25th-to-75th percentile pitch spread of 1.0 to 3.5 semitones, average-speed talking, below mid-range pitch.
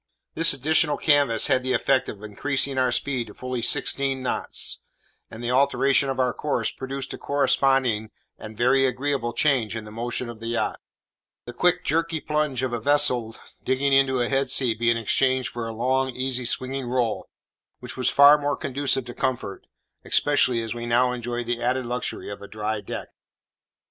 Yes: narrow, 2.5 semitones; average, 180 wpm; low, 130 Hz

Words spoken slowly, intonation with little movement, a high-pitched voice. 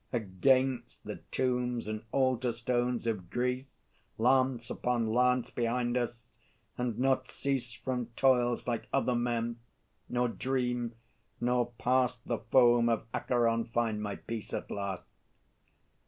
No: slow, 125 wpm; narrow, 1.4 semitones; low, 120 Hz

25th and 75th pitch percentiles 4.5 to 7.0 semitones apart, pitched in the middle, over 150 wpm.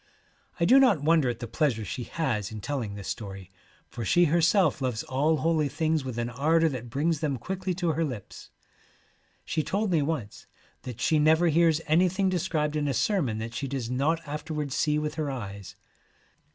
Yes: average, 5.0 semitones; medium, 150 Hz; average, 190 wpm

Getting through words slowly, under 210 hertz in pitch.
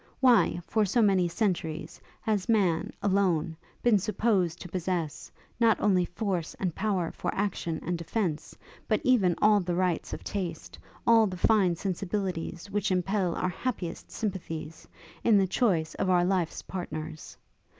No: average, 150 wpm; medium, 185 Hz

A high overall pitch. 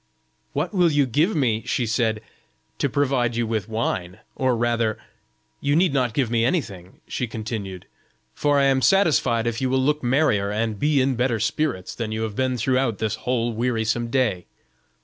No: low, 120 Hz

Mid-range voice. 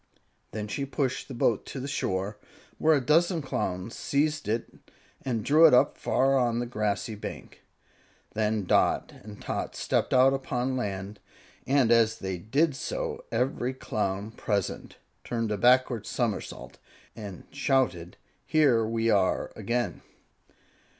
No: low, 120 Hz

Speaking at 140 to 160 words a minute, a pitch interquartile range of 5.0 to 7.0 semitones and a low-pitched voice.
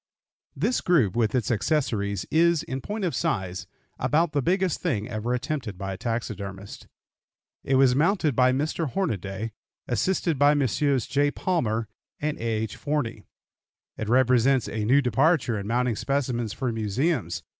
Yes: average, 150 wpm; wide, 5.4 semitones; low, 125 Hz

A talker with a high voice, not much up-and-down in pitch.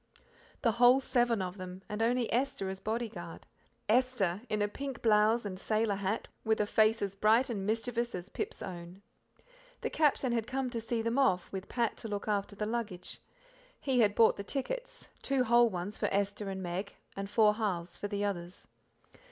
No: high, 215 Hz; average, 3.2 semitones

